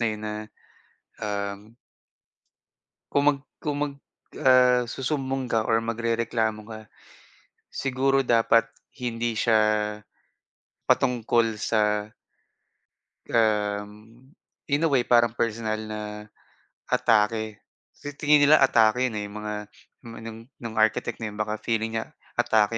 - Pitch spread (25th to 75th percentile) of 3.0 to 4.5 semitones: No, narrow, 2.6 semitones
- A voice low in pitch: Yes, low, 115 Hz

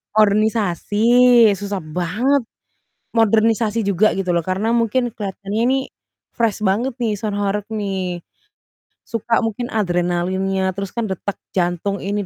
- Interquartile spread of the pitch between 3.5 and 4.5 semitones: No, average, 3.0 semitones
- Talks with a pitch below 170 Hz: No, high, 205 Hz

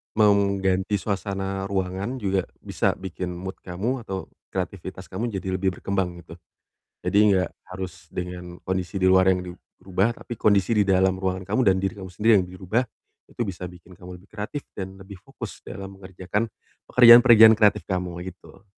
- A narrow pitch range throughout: Yes, narrow, 1.8 semitones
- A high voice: No, very low, 95 Hz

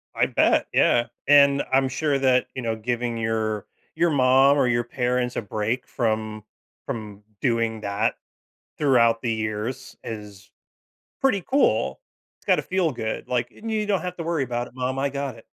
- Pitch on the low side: Yes, low, 125 Hz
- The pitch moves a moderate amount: Yes, average, 3.8 semitones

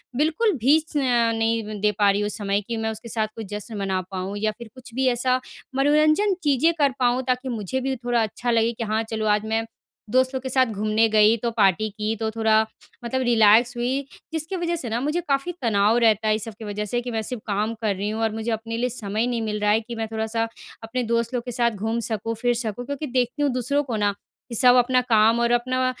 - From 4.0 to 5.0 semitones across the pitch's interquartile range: No, average, 2.8 semitones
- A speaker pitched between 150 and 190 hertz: No, high, 230 Hz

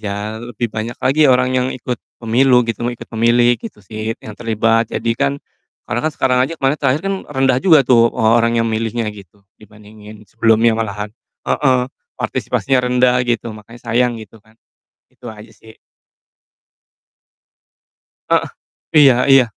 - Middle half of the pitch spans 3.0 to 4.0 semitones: No, narrow, 2.5 semitones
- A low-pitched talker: Yes, low, 115 Hz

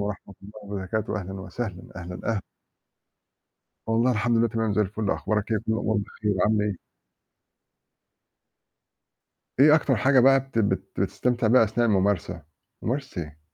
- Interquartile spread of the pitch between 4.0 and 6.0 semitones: No, average, 3.0 semitones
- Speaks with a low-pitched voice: Yes, low, 110 Hz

